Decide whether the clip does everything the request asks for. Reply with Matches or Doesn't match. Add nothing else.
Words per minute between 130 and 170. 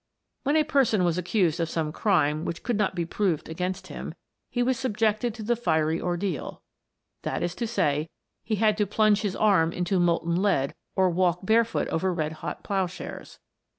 Doesn't match